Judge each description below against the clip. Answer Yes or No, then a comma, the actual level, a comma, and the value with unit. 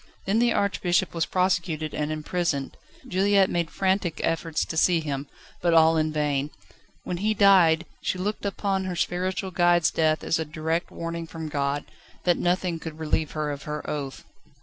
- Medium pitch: Yes, medium, 165 Hz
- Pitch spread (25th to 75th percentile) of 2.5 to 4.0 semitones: Yes, average, 2.9 semitones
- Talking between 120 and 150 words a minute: No, average, 170 wpm